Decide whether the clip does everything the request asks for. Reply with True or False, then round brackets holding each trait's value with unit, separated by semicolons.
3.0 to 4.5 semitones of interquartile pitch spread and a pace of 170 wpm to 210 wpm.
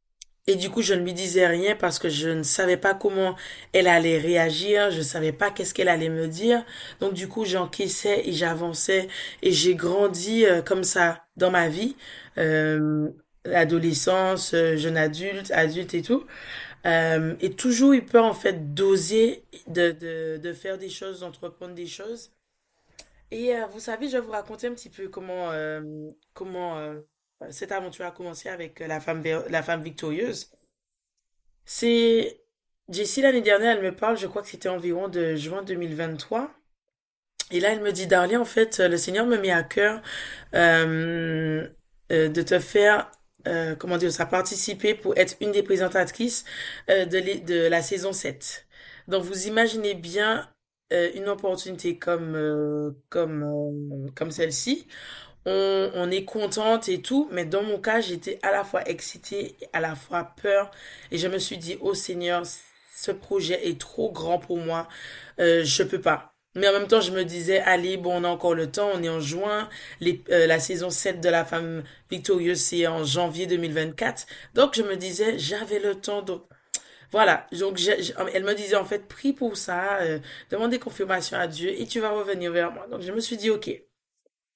True (3.7 semitones; 185 wpm)